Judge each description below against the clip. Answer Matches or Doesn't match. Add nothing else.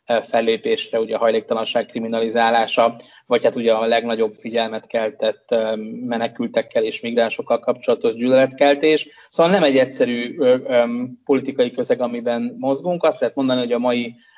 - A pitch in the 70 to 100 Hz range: Doesn't match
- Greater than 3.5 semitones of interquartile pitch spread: Doesn't match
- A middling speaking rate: Matches